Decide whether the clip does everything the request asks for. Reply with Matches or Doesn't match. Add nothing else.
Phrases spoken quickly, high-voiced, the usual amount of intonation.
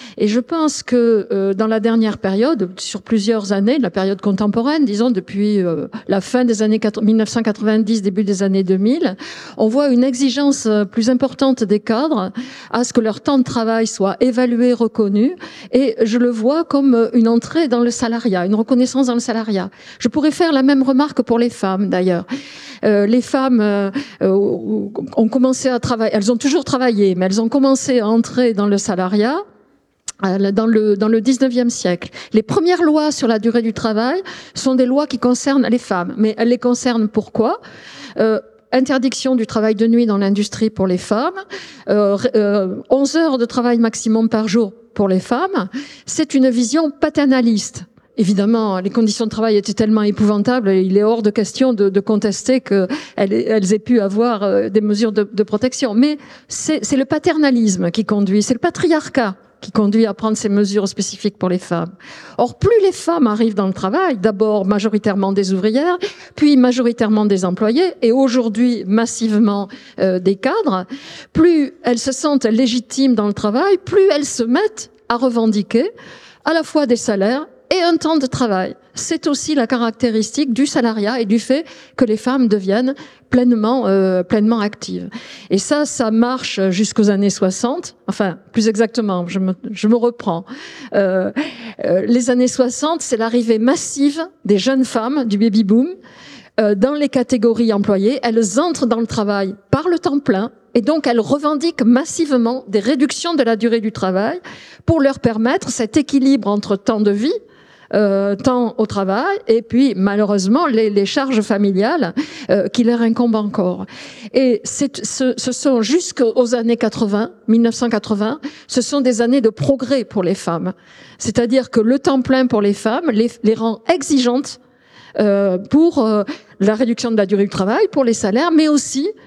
Doesn't match